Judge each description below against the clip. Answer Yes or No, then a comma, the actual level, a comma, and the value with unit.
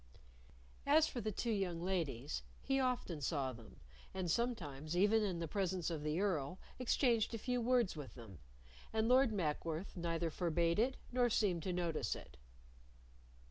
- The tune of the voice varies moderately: No, wide, 6.2 semitones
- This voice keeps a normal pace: Yes, average, 160 wpm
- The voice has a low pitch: No, medium, 180 Hz